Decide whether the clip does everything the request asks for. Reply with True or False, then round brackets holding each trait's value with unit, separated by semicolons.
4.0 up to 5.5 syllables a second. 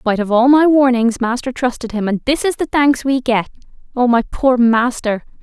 True (5.0 syllables/s)